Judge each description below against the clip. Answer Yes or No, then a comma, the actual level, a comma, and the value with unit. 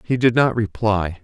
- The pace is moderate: Yes, average, 195 wpm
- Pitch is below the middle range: Yes, low, 110 Hz